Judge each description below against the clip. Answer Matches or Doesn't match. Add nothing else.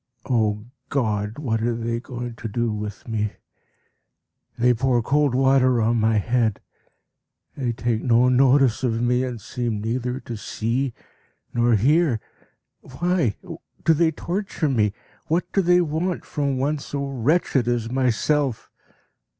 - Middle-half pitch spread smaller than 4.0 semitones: Matches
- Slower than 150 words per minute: Matches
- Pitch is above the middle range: Doesn't match